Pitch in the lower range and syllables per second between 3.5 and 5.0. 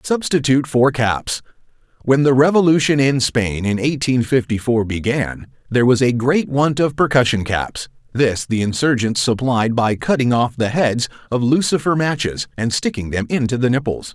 Yes: low, 125 Hz; 4.8 syllables/s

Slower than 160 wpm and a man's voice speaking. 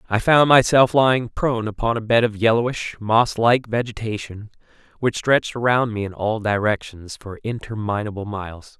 Yes: average, 150 wpm; male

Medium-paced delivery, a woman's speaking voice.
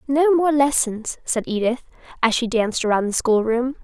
Yes: average, 170 wpm; female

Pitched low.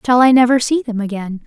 No: high, 240 Hz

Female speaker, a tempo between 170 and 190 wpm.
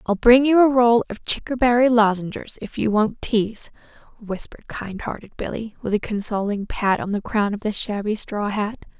Yes: female; average, 185 wpm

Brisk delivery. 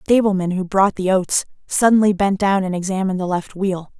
Yes: fast, 210 wpm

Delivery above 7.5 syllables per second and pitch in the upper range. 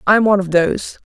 Yes: 7.9 syllables/s; high, 195 Hz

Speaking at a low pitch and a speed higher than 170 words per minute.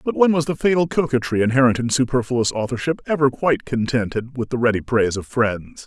Yes: low, 125 Hz; average, 195 wpm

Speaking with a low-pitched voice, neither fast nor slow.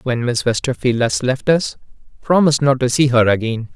Yes: low, 130 Hz; average, 190 wpm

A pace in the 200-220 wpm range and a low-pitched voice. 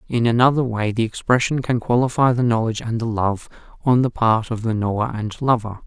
Yes: fast, 205 wpm; low, 115 Hz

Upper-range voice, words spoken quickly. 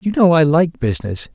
No: medium, 155 Hz; fast, 220 wpm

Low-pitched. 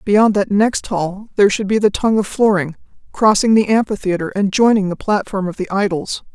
No: high, 200 Hz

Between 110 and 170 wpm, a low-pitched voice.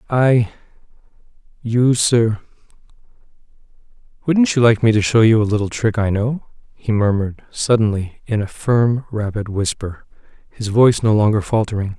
Yes: average, 140 wpm; low, 110 Hz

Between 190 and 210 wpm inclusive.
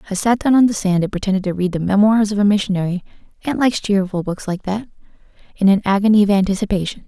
Yes: fast, 205 wpm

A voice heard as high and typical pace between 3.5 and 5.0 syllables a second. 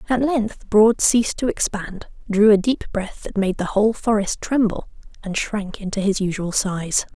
Yes: high, 210 Hz; 4.6 syllables/s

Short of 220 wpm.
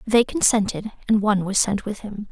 Yes: fast, 205 wpm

